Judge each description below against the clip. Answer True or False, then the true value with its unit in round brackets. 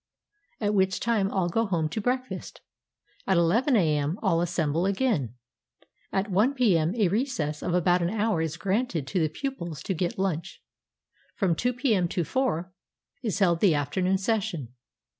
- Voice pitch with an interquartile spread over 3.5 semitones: True (4.8 semitones)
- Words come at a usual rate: True (160 wpm)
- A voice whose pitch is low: False (185 Hz)